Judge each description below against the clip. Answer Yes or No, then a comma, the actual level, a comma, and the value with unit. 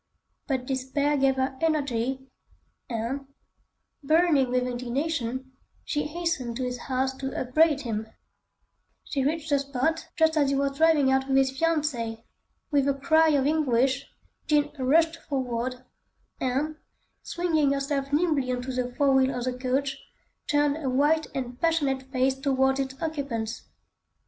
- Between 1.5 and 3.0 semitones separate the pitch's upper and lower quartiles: Yes, narrow, 2.6 semitones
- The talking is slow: No, average, 145 wpm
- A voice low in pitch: No, very high, 270 Hz